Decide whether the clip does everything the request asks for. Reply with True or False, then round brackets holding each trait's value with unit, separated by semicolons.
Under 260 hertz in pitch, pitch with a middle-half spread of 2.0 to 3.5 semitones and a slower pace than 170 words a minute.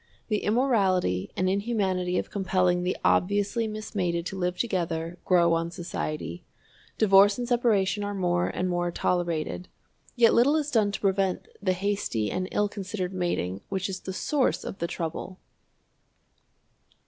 True (185 Hz; 2.7 semitones; 150 wpm)